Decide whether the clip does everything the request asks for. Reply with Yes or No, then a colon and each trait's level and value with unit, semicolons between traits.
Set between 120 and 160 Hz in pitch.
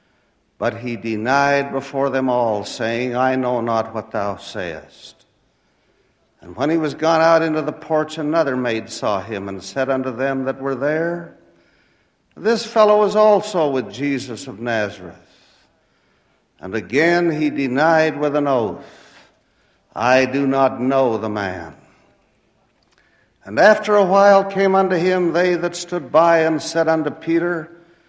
Yes: medium, 140 Hz